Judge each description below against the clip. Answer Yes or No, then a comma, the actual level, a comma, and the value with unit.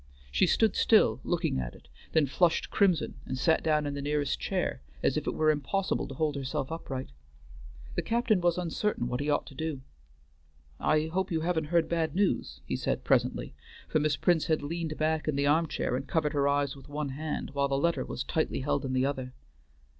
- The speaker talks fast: Yes, fast, 210 wpm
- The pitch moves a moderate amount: Yes, average, 3.0 semitones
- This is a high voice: No, medium, 150 Hz